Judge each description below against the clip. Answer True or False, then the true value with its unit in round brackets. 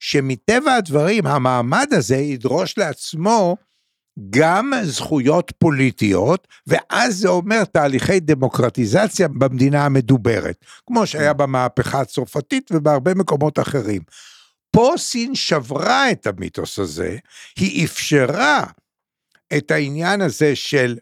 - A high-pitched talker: False (150 Hz)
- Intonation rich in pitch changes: True (6.1 semitones)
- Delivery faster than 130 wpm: False (100 wpm)